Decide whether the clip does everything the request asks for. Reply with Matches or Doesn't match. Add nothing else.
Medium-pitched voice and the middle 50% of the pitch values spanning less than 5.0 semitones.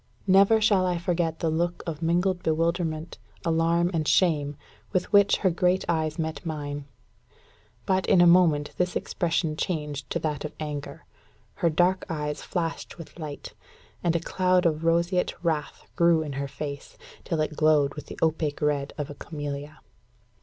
Matches